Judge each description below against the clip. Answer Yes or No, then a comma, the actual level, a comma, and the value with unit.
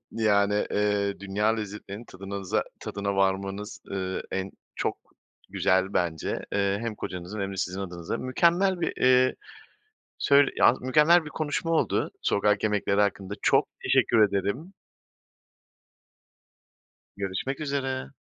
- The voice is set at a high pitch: No, low, 100 Hz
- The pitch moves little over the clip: No, average, 4.8 semitones